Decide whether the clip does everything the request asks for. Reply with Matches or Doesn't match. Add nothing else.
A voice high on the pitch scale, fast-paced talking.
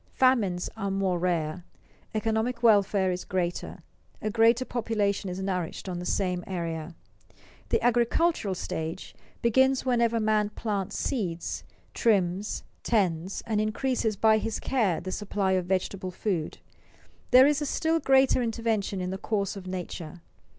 Doesn't match